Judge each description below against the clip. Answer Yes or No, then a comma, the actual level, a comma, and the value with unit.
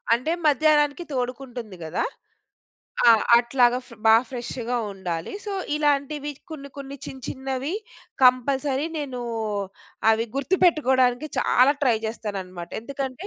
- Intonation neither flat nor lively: Yes, average, 3.0 semitones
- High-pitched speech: Yes, very high, 260 Hz